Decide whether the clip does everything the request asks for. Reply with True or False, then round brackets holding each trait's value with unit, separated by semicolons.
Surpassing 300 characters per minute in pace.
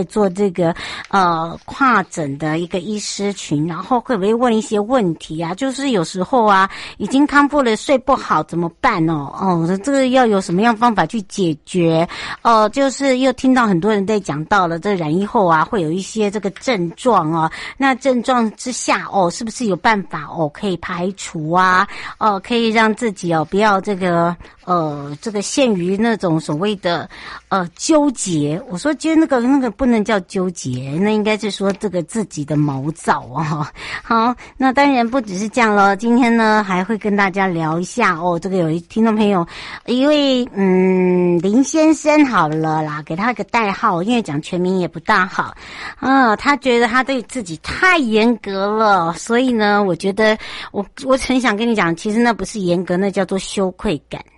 False (270 characters per minute)